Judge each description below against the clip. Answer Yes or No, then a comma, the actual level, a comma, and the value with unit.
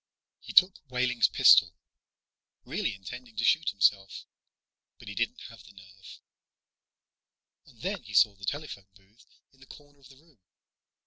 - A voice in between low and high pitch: No, low, 115 Hz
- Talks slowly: No, average, 150 wpm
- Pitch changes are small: No, average, 5.3 semitones